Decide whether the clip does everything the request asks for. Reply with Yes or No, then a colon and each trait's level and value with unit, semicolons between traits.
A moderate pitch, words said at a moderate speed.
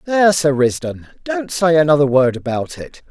Yes: medium, 150 Hz; average, 175 wpm